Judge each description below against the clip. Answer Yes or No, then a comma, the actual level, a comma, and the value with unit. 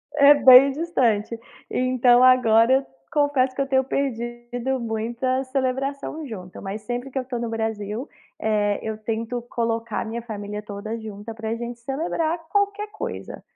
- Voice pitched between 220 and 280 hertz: Yes, high, 240 Hz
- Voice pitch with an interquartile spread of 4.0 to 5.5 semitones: No, average, 3.2 semitones